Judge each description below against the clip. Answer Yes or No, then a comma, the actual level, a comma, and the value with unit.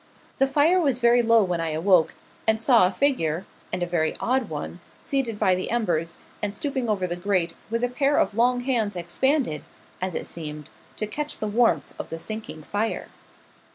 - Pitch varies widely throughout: Yes, wide, 6.1 semitones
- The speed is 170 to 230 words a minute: Yes, average, 190 wpm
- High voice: Yes, high, 215 Hz